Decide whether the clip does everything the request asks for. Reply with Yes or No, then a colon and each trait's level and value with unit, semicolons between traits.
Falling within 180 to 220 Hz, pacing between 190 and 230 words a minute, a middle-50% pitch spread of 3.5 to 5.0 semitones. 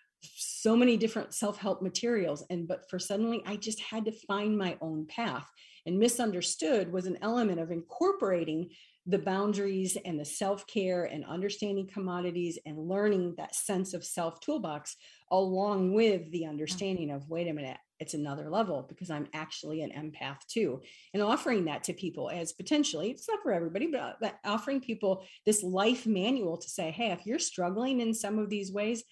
No: high, 190 Hz; average, 175 wpm; average, 4.1 semitones